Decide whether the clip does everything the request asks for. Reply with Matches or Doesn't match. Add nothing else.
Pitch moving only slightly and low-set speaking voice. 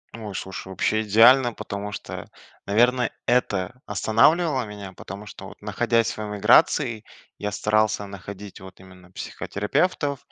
Doesn't match